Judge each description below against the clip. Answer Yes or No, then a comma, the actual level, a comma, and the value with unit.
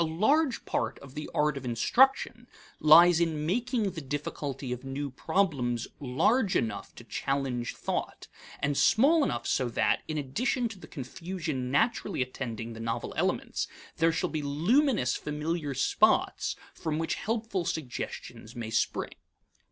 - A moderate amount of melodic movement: No, wide, 6.8 semitones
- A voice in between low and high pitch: Yes, medium, 150 Hz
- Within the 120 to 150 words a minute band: Yes, average, 145 wpm